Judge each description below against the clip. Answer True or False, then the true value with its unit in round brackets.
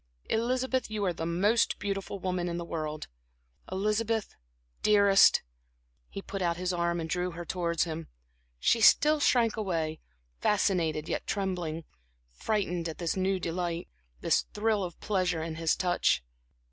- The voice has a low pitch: False (180 Hz)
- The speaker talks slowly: False (145 wpm)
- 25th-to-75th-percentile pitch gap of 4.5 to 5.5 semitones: False (3.5 semitones)